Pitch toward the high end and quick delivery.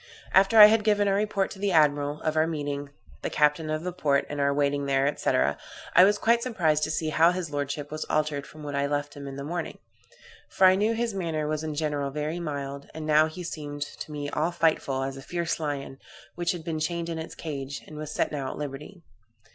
No: medium, 155 Hz; fast, 230 wpm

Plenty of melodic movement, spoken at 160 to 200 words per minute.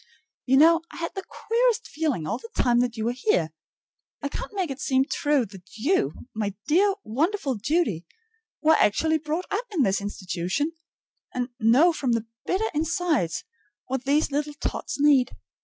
Yes: wide, 6.4 semitones; average, 170 wpm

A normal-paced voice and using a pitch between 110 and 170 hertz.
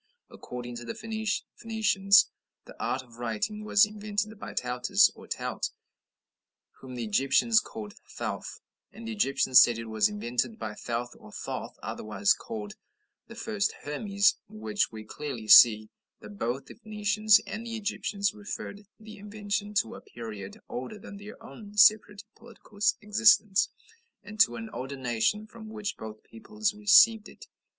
No: average, 150 wpm; high, 205 Hz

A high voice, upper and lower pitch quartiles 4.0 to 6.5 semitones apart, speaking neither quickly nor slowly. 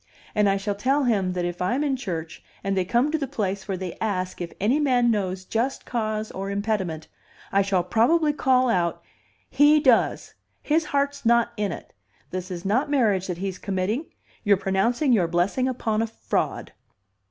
Yes: high, 210 Hz; average, 5.3 semitones; average, 185 wpm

